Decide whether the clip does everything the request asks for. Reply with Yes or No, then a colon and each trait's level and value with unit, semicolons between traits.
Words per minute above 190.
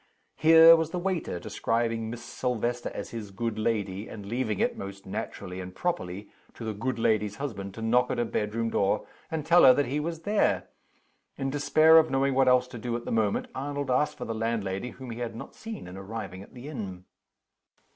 Yes: fast, 205 wpm